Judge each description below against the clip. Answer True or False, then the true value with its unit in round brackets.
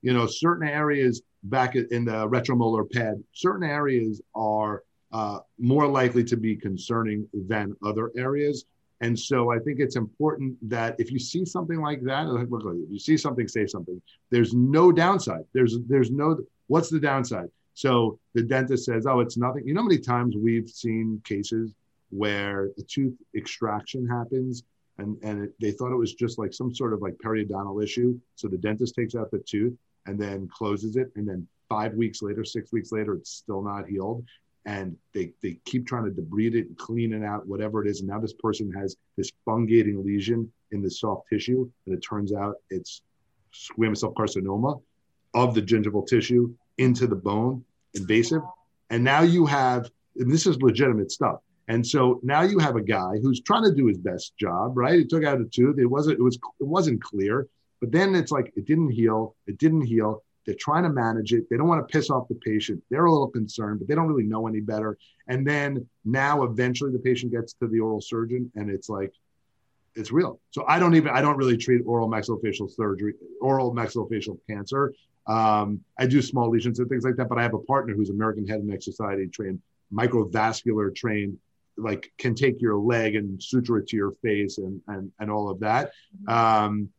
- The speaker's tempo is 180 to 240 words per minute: True (200 wpm)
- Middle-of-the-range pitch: False (115 Hz)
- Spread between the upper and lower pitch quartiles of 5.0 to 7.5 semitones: False (3.3 semitones)